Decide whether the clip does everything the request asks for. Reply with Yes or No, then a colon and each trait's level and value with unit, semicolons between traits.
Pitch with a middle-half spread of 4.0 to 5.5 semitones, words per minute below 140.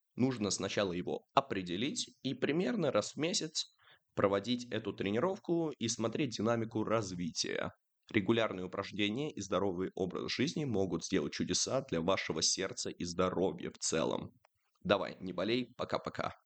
Yes: average, 4.3 semitones; average, 130 wpm